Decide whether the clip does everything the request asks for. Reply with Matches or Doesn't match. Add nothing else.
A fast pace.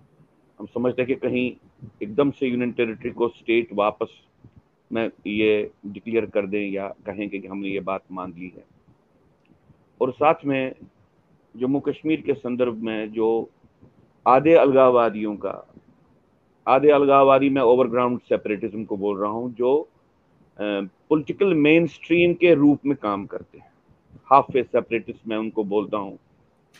Doesn't match